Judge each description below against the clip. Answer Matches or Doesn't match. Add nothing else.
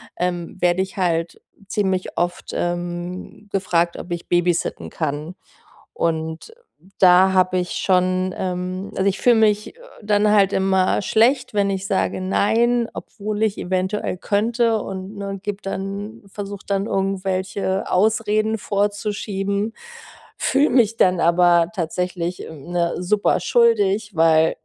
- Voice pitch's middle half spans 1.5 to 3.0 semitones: Matches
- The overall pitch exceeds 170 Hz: Matches